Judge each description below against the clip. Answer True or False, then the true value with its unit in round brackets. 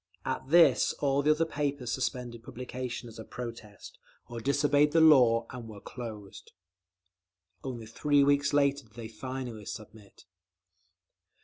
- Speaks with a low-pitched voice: True (125 Hz)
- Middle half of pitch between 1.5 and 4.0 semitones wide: True (3.6 semitones)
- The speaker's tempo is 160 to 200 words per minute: False (135 wpm)